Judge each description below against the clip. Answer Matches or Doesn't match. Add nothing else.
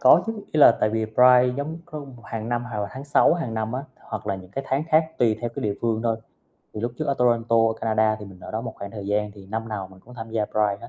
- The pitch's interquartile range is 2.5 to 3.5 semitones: Matches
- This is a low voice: Matches